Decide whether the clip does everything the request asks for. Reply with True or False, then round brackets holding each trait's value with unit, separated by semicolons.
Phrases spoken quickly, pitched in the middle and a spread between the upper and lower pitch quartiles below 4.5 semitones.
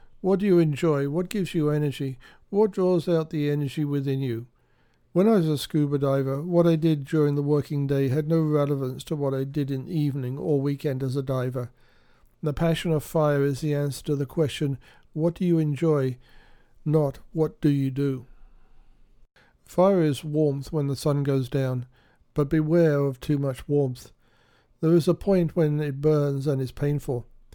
False (185 wpm; 145 Hz; 2.7 semitones)